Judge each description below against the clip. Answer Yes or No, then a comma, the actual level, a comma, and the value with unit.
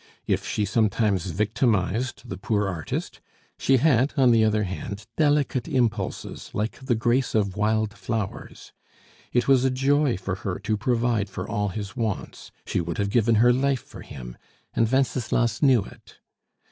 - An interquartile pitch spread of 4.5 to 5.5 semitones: No, average, 3.7 semitones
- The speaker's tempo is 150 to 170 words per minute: Yes, average, 160 wpm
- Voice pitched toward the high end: No, low, 110 Hz